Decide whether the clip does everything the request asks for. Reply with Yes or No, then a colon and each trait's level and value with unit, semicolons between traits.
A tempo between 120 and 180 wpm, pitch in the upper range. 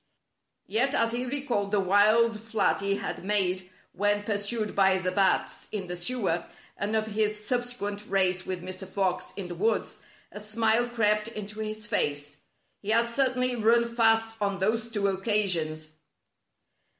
Yes: average, 155 wpm; high, 210 Hz